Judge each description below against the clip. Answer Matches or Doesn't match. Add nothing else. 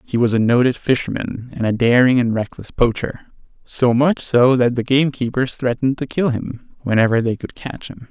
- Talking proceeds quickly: Doesn't match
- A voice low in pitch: Matches